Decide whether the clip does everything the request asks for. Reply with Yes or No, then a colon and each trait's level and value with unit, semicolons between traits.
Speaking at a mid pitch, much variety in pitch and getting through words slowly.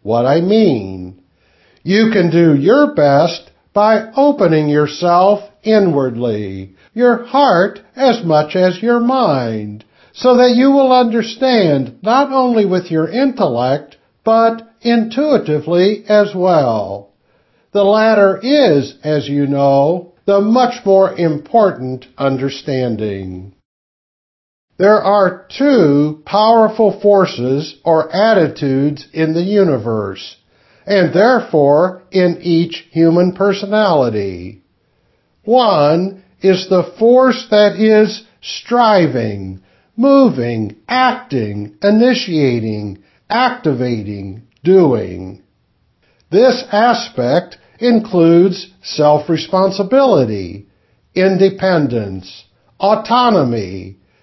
Yes: medium, 180 Hz; wide, 9.0 semitones; slow, 85 wpm